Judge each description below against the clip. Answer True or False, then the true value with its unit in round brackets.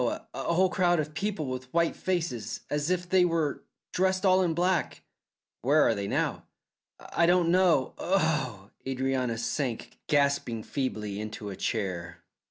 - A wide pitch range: True (6.9 semitones)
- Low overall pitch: False (150 Hz)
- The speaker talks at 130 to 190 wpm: True (150 wpm)